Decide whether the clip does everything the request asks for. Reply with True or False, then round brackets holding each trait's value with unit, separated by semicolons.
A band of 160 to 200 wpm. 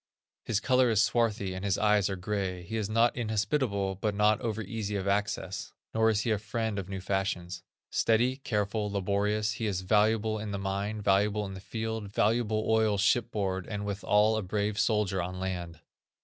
True (185 wpm)